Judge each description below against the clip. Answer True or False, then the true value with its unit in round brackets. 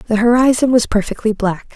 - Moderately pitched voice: False (225 Hz)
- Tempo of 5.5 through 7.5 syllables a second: False (5.3 syllables/s)